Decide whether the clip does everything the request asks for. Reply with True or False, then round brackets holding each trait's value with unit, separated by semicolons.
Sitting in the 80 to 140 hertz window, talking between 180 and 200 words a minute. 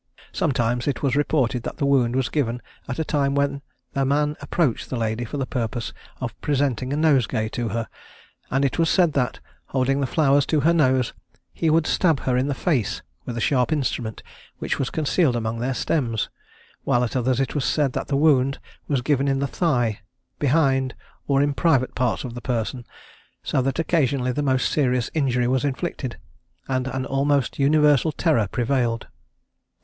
True (135 Hz; 185 wpm)